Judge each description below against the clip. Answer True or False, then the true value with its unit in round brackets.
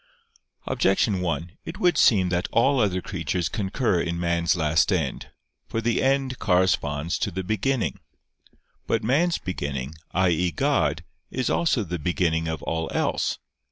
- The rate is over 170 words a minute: False (145 wpm)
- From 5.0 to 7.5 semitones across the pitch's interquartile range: True (5.3 semitones)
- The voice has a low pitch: True (90 Hz)